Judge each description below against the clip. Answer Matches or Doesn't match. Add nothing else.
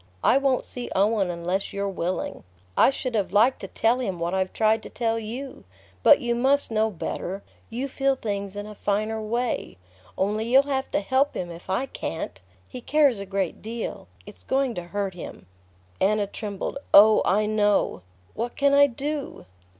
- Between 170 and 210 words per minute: Matches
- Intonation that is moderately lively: Matches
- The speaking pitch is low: Doesn't match